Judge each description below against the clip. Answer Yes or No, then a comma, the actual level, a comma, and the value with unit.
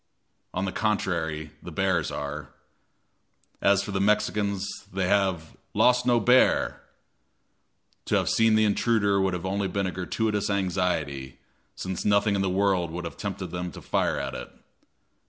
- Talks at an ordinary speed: Yes, average, 155 wpm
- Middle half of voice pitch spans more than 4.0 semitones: No, narrow, 2.5 semitones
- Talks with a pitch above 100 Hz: No, very low, 95 Hz